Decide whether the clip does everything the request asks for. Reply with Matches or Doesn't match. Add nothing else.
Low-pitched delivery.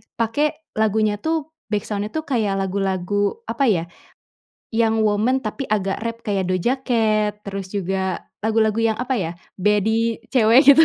Doesn't match